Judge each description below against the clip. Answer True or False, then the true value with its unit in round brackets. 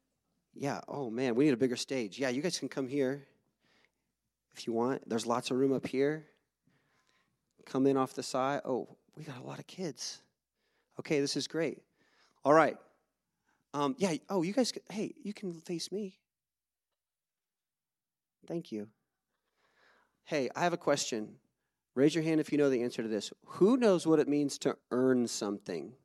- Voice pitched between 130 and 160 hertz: True (140 Hz)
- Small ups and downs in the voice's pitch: False (4.2 semitones)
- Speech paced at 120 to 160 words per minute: False (175 wpm)